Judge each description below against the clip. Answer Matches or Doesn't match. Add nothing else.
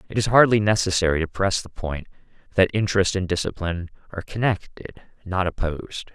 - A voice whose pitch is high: Doesn't match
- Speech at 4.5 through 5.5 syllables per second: Doesn't match